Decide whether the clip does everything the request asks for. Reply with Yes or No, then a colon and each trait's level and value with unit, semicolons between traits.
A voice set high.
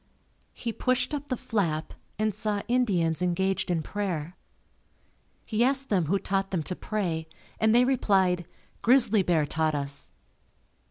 Yes: high, 195 Hz